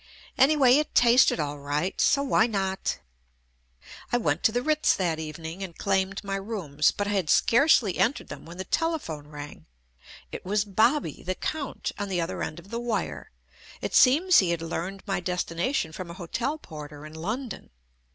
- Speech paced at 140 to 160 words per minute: No, average, 180 wpm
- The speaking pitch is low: No, high, 195 Hz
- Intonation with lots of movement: Yes, wide, 6.5 semitones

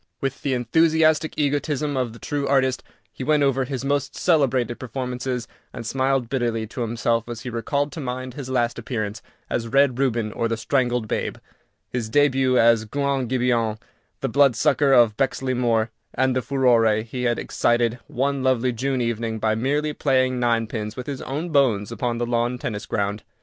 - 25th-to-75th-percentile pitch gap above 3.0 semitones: No, average, 2.7 semitones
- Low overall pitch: Yes, low, 125 Hz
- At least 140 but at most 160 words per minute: No, average, 175 wpm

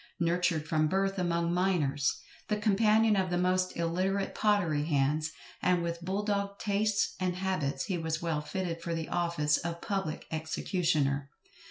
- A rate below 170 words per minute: Yes, average, 155 wpm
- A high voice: No, medium, 175 Hz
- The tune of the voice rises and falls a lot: No, average, 3.3 semitones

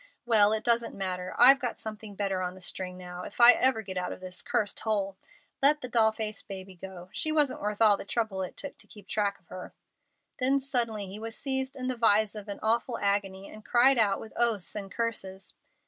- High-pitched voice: Yes, high, 215 Hz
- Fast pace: Yes, fast, 225 wpm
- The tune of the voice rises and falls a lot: No, average, 3.5 semitones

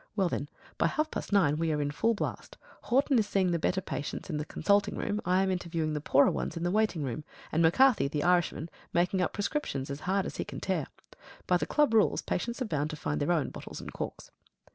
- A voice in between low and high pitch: Yes, medium, 175 Hz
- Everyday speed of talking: No, fast, 235 wpm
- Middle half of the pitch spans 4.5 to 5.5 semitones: Yes, average, 5.1 semitones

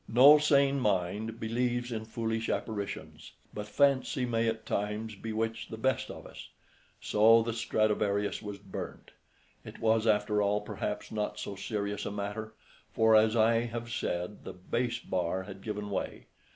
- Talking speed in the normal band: Yes, average, 155 wpm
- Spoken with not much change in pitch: Yes, narrow, 2.0 semitones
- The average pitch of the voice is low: Yes, low, 110 Hz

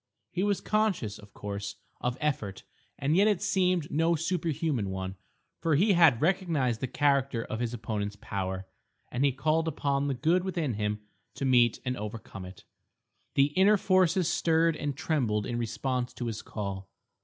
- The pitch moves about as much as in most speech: No, wide, 7.2 semitones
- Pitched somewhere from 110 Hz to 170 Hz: Yes, low, 135 Hz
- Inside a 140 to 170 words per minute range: Yes, average, 165 wpm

